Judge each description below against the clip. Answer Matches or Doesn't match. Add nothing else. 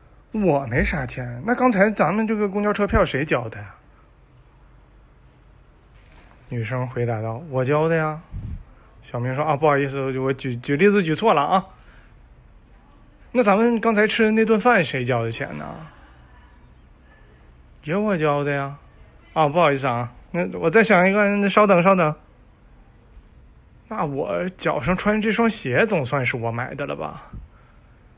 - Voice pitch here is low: Doesn't match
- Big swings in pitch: Matches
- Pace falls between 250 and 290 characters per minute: Doesn't match